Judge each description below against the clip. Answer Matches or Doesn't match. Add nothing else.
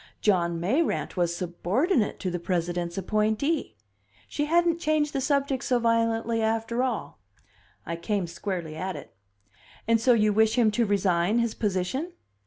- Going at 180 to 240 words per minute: Doesn't match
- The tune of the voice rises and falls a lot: Matches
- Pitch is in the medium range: Doesn't match